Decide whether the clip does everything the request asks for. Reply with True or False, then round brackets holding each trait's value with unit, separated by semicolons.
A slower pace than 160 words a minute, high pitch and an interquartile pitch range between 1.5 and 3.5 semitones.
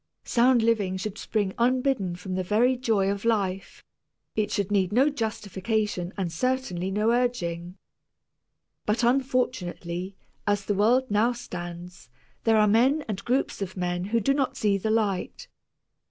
False (150 wpm; 210 Hz; 4.4 semitones)